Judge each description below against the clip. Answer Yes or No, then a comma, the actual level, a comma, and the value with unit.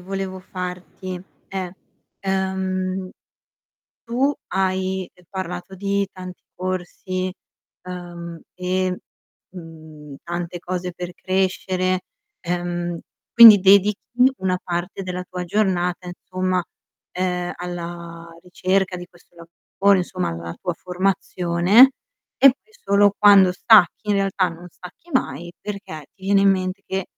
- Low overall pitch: No, medium, 185 Hz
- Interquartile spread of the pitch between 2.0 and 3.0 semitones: No, narrow, 1.4 semitones